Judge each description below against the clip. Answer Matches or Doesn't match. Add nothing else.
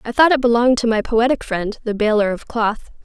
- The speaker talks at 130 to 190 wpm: Doesn't match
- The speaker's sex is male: Doesn't match